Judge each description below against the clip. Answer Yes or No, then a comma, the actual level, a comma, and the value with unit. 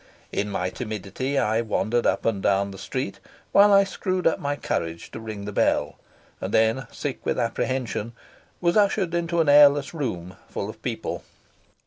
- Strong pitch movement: Yes, wide, 7.2 semitones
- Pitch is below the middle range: Yes, low, 125 Hz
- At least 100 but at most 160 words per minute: No, average, 170 wpm